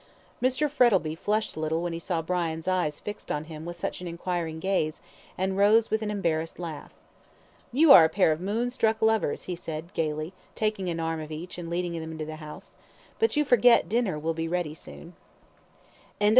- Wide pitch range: No, average, 4.8 semitones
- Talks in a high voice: No, medium, 175 Hz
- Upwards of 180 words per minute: Yes, average, 200 wpm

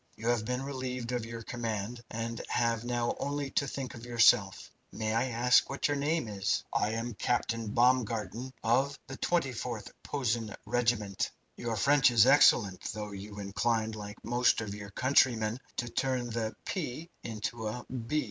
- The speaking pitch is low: Yes, low, 120 Hz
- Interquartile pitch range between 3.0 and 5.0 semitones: No, narrow, 2.5 semitones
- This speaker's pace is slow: No, average, 165 wpm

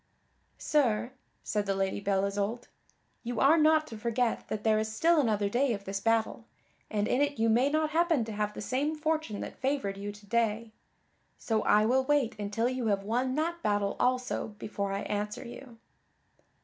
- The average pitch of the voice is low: No, high, 225 Hz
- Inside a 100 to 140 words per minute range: No, average, 190 wpm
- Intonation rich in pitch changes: No, average, 4.3 semitones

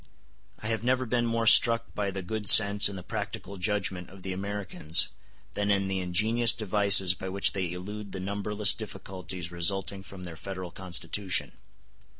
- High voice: No, low, 100 Hz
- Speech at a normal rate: Yes, average, 165 wpm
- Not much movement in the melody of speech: Yes, narrow, 2.2 semitones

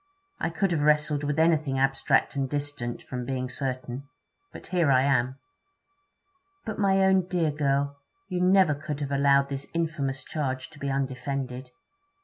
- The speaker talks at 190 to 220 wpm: No, average, 155 wpm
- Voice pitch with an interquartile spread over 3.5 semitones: No, average, 2.9 semitones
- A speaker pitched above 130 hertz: Yes, medium, 140 Hz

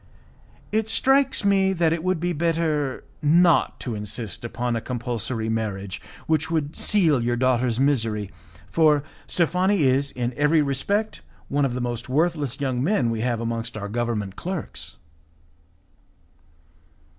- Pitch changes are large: Yes, wide, 5.9 semitones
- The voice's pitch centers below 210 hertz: Yes, low, 135 Hz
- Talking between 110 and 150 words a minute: Yes, average, 140 wpm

